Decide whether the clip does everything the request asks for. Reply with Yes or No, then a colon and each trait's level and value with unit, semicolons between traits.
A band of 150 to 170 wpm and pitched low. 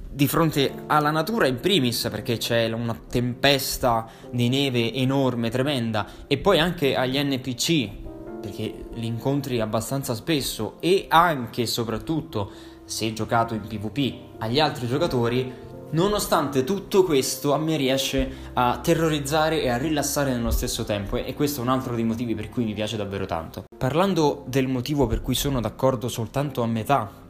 Yes: average, 160 wpm; low, 130 Hz